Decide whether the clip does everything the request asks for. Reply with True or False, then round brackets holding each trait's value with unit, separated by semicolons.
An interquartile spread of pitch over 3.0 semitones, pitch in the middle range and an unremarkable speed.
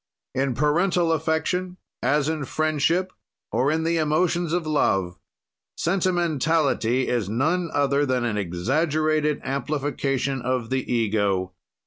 False (4.2 semitones; 145 Hz; 115 wpm)